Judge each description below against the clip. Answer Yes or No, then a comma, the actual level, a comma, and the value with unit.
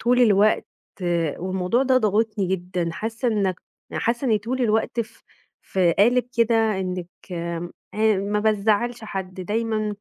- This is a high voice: Yes, high, 210 Hz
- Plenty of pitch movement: No, average, 3.6 semitones